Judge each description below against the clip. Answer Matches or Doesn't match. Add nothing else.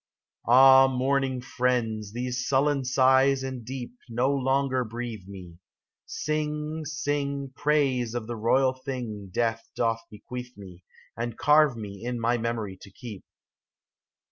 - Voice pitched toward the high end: Doesn't match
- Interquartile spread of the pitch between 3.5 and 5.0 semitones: Doesn't match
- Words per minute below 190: Matches